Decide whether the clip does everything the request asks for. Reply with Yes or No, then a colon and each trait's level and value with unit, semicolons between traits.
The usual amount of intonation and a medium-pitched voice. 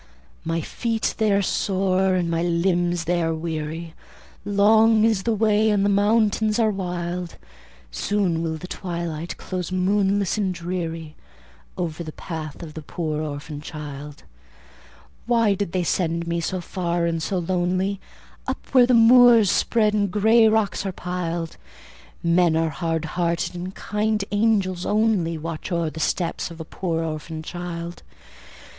Yes: average, 3.6 semitones; medium, 180 Hz